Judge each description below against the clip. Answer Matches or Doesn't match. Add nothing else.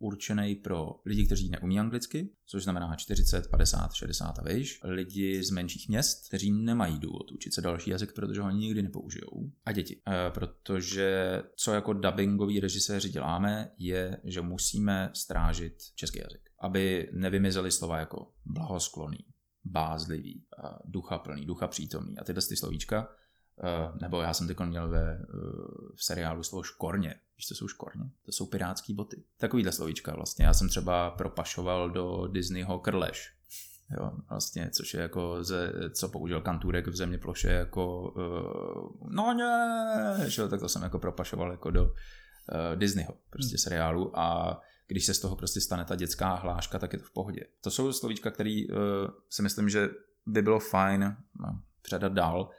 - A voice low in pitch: Matches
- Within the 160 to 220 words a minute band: Matches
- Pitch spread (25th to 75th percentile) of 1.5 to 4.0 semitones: Matches